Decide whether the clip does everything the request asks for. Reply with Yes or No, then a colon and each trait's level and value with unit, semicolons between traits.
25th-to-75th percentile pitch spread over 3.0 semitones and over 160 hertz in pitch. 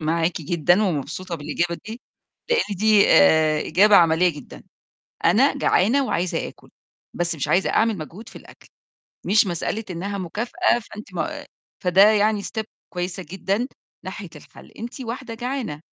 Yes: average, 4.4 semitones; high, 190 Hz